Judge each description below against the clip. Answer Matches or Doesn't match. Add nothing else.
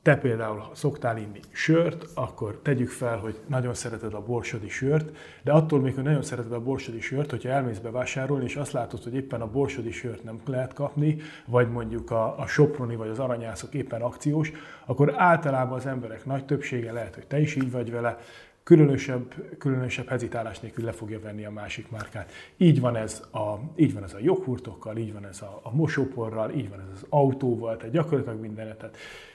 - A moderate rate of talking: Doesn't match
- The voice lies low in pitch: Matches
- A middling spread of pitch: Matches